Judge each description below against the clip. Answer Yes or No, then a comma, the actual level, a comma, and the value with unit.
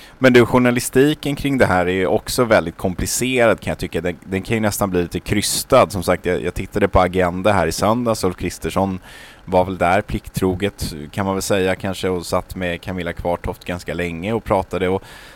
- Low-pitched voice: Yes, very low, 95 Hz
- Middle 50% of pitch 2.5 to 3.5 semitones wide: Yes, average, 3.2 semitones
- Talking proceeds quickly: Yes, fast, 205 wpm